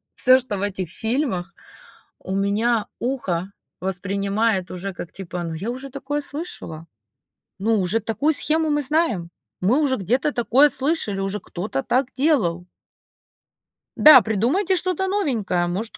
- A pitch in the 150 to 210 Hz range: No, high, 225 Hz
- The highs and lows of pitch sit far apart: Yes, wide, 6.5 semitones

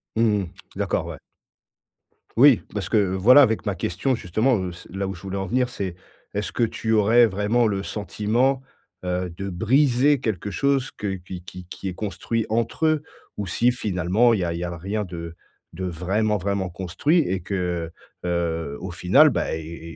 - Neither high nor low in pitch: No, low, 100 Hz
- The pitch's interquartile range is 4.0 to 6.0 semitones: Yes, average, 4.4 semitones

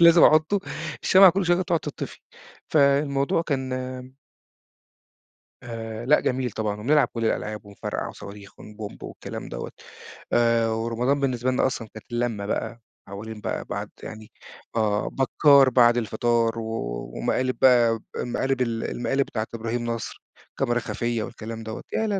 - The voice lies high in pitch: No, low, 120 Hz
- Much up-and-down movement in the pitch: No, average, 3.5 semitones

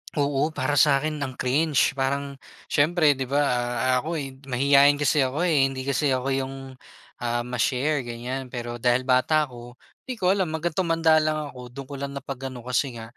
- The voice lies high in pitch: No, low, 135 Hz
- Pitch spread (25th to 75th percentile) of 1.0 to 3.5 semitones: Yes, average, 2.8 semitones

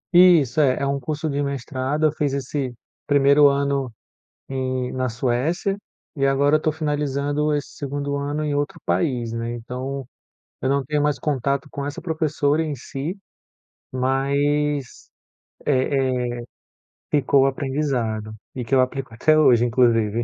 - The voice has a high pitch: No, medium, 140 Hz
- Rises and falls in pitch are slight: Yes, narrow, 2.3 semitones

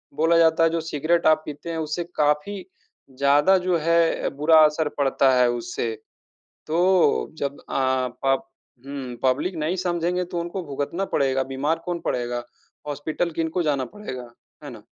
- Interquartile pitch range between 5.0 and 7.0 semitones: No, average, 3.8 semitones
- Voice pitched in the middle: Yes, medium, 155 Hz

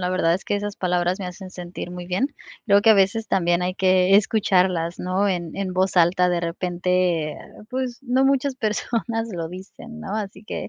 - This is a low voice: No, medium, 185 Hz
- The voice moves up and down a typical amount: Yes, average, 3.1 semitones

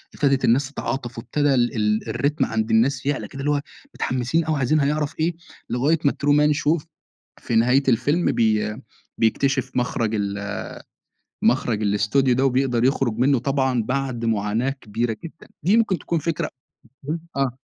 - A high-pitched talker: No, low, 130 Hz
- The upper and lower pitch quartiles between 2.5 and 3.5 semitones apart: No, average, 3.9 semitones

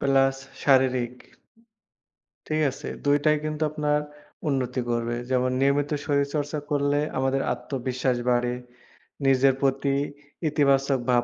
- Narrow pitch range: Yes, narrow, 2.0 semitones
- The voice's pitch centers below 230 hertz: Yes, low, 135 Hz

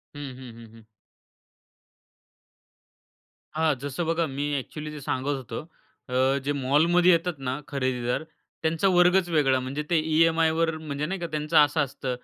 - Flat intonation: No, average, 3.7 semitones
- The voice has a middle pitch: Yes, medium, 150 Hz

